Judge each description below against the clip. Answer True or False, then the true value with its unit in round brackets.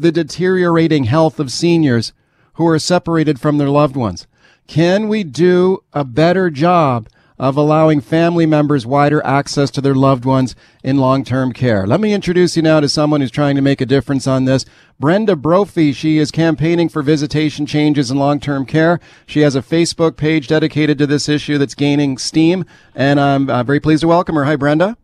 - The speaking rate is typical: True (190 wpm)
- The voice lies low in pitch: False (150 Hz)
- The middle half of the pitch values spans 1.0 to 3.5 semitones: True (2.9 semitones)